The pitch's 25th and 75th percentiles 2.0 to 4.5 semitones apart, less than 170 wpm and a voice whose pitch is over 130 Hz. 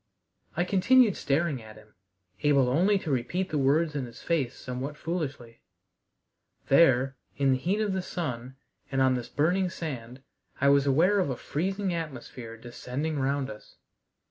No: average, 5.0 semitones; average, 160 wpm; medium, 140 Hz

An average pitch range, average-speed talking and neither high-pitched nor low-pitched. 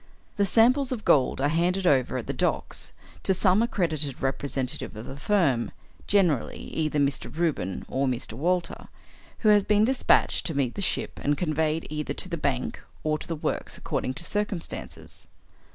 No: wide, 5.8 semitones; average, 170 wpm; medium, 160 Hz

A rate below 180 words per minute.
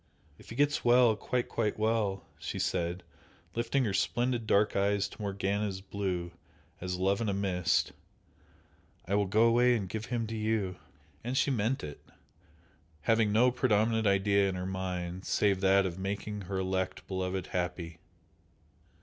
Yes: average, 160 wpm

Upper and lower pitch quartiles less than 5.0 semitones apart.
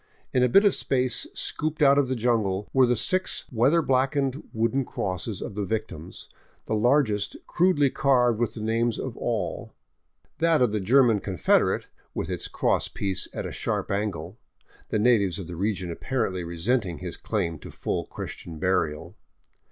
No: wide, 5.5 semitones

